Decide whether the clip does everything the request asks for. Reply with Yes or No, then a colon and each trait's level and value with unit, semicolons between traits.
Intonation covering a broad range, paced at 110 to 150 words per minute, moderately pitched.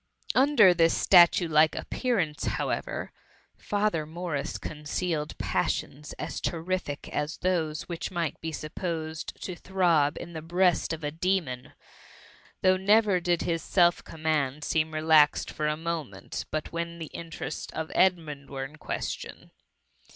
No: average, 2.8 semitones; slow, 135 wpm; medium, 165 Hz